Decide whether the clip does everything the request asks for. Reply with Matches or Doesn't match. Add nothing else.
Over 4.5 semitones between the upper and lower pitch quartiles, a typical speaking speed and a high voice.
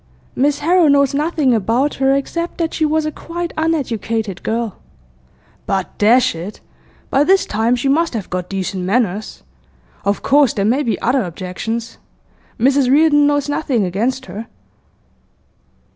Matches